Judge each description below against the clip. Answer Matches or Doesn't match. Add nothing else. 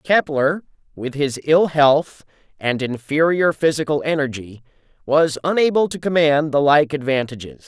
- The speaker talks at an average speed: Doesn't match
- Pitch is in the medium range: Matches